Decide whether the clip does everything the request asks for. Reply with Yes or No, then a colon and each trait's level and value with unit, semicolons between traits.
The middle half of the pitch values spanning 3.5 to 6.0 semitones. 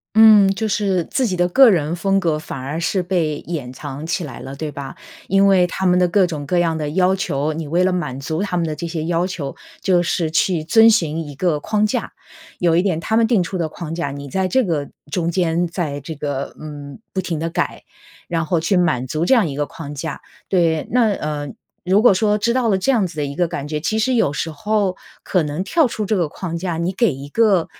Yes: average, 4.1 semitones